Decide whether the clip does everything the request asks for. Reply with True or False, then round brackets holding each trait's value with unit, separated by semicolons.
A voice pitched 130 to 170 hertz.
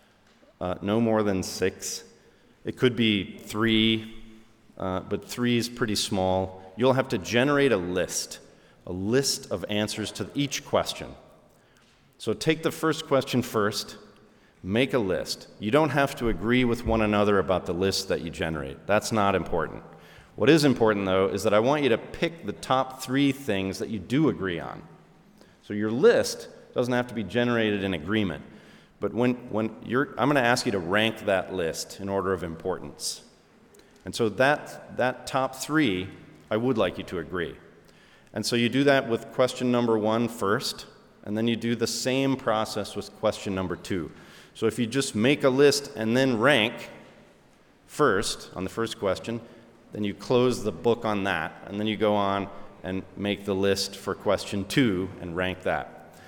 False (110 Hz)